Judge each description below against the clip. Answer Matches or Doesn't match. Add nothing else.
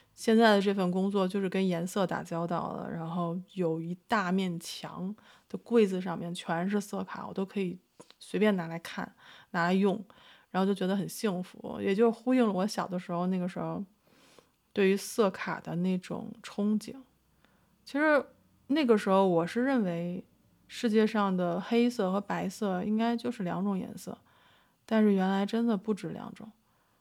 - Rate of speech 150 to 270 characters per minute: Matches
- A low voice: Doesn't match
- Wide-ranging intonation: Doesn't match